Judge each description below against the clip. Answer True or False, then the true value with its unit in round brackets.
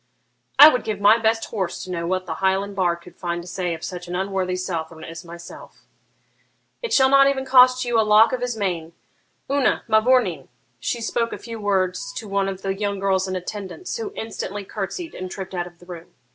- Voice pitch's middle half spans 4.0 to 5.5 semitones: True (4.3 semitones)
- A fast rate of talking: True (215 wpm)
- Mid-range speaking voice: False (195 Hz)